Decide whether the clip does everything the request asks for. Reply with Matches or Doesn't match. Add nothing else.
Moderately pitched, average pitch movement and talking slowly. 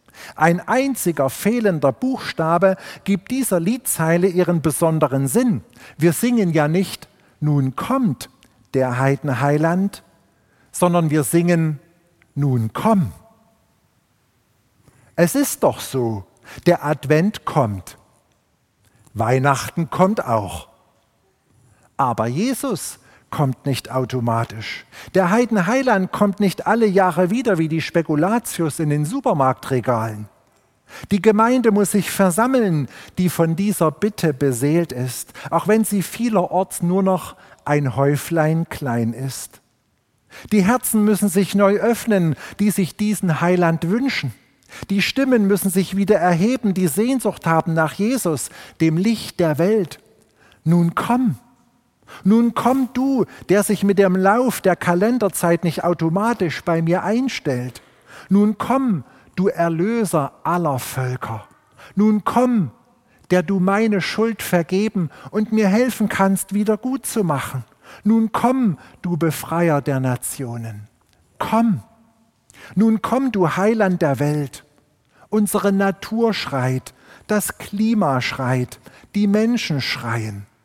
Doesn't match